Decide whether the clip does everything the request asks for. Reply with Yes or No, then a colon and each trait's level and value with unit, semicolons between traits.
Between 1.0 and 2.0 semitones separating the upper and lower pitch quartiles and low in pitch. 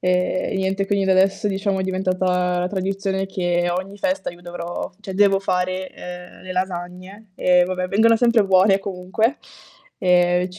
No: narrow, 1.3 semitones; medium, 185 Hz